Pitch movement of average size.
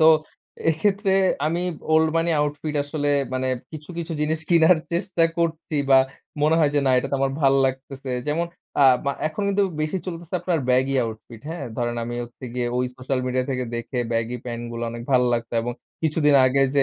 Yes: average, 4.3 semitones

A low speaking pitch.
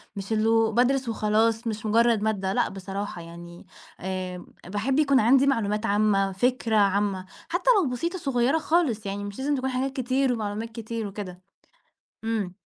No: high, 220 Hz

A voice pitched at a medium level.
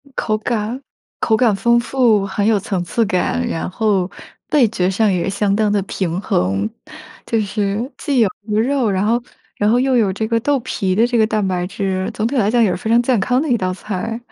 No: high, 215 Hz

